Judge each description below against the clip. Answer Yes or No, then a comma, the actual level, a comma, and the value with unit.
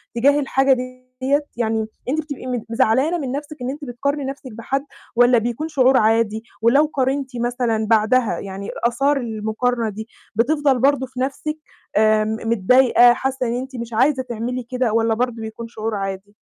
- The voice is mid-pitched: No, high, 245 Hz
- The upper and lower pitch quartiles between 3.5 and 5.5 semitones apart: No, average, 3.1 semitones